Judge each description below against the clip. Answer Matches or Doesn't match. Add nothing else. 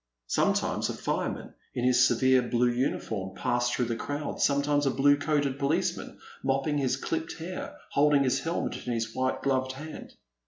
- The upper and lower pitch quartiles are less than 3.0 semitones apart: Matches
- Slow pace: Doesn't match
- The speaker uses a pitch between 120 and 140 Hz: Matches